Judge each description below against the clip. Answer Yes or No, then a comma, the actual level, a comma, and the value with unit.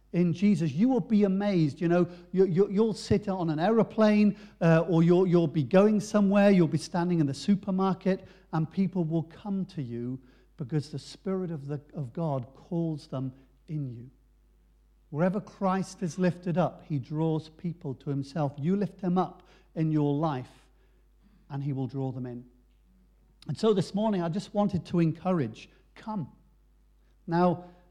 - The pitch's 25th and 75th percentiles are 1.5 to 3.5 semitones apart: No, average, 4.7 semitones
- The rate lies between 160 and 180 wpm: Yes, average, 170 wpm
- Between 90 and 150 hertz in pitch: No, medium, 170 Hz